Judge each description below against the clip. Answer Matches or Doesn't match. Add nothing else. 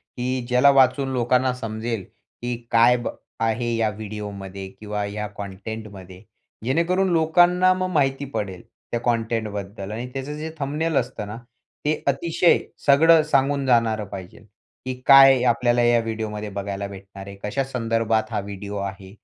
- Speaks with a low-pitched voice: Matches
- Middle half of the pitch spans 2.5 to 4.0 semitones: Doesn't match